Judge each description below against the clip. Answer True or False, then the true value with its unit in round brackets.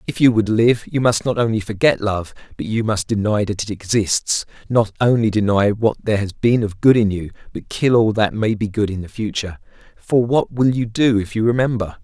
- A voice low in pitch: True (110 Hz)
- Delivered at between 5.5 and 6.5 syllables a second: False (5.3 syllables/s)